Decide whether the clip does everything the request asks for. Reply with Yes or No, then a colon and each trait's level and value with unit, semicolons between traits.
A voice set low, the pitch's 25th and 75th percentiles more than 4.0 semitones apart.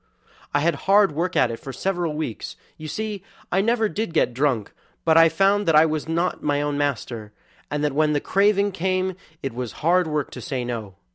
No: medium, 155 Hz; average, 4.9 semitones